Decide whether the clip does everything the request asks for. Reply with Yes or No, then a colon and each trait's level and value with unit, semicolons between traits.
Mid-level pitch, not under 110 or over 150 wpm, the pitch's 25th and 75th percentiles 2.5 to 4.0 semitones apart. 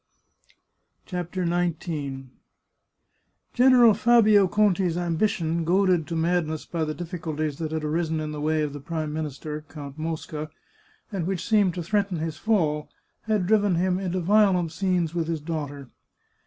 Yes: medium, 170 Hz; average, 145 wpm; average, 3.3 semitones